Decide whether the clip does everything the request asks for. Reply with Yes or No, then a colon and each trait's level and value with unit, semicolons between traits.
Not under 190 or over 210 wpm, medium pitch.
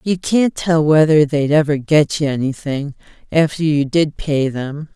No: average, 170 wpm; medium, 150 Hz